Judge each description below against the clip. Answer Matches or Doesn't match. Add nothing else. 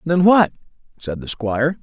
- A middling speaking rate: Matches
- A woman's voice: Doesn't match